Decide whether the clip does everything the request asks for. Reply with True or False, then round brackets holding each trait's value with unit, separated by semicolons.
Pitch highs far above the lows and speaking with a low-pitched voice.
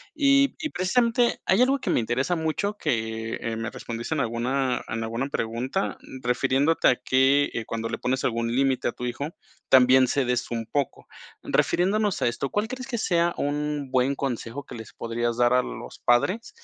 True (6.3 semitones; 130 Hz)